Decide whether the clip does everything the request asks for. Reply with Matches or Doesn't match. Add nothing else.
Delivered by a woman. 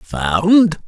Doesn't match